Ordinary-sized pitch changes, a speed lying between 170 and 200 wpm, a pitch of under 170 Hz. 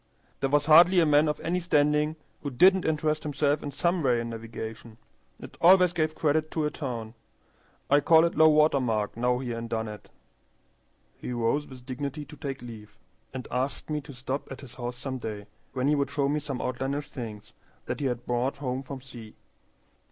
Yes: average, 3.7 semitones; average, 195 wpm; medium, 140 Hz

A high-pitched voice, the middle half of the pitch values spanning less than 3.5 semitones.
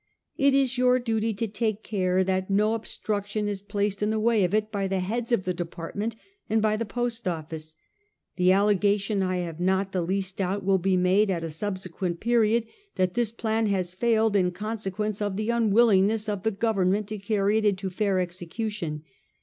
Yes: high, 205 Hz; average, 2.8 semitones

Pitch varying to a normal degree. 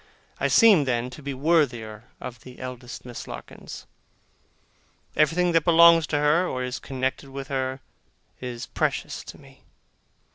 Yes: average, 4.0 semitones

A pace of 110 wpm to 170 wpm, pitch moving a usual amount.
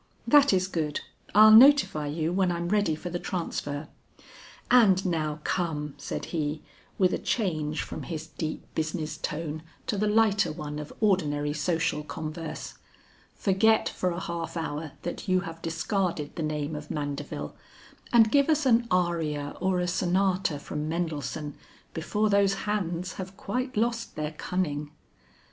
Yes: average, 150 wpm; average, 4.3 semitones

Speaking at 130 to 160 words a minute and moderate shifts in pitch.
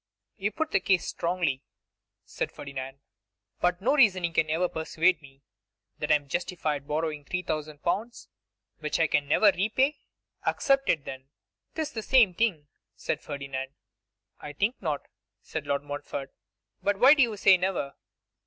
No: average, 155 wpm; wide, 5.8 semitones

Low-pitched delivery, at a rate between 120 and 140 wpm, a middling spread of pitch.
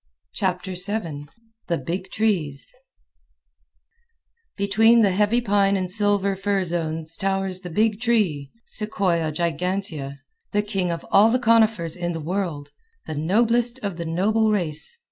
No: high, 190 Hz; slow, 135 wpm; average, 3.9 semitones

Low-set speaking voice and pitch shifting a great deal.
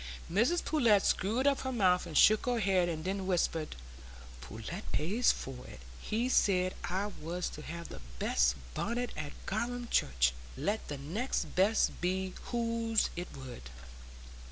No: high, 190 Hz; wide, 6.2 semitones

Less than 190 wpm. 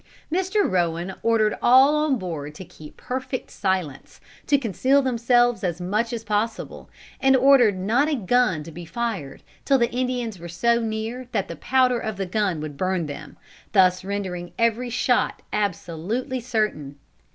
Yes: average, 160 wpm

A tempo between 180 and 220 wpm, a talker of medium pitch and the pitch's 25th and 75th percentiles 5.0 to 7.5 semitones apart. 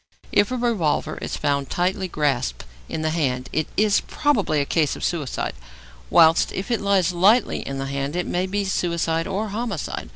Yes: average, 185 wpm; medium, 170 Hz; average, 5.3 semitones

